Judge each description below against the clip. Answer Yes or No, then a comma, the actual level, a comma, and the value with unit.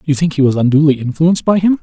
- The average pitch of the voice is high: No, medium, 155 Hz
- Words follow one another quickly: Yes, fast, 265 wpm